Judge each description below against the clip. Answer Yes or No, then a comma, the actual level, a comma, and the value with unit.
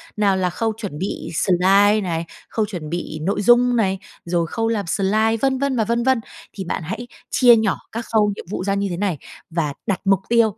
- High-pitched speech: Yes, high, 205 Hz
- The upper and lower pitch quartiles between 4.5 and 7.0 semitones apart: No, average, 3.8 semitones